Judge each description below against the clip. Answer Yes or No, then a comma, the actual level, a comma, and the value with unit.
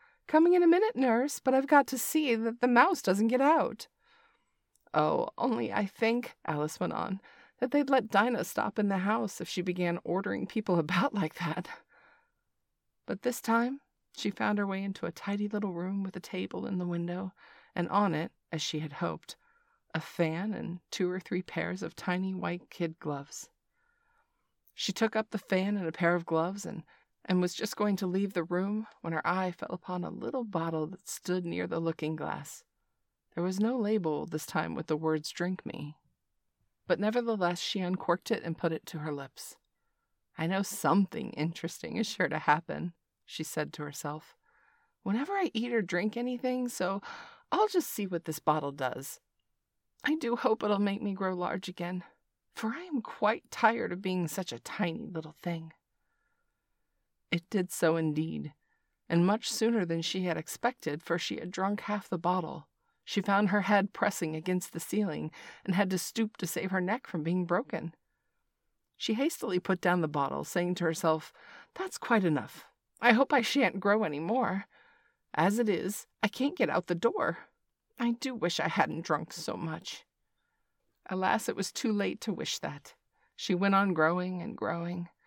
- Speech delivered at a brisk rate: No, average, 185 wpm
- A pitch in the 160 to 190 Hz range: Yes, medium, 185 Hz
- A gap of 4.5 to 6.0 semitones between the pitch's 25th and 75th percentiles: Yes, average, 5.2 semitones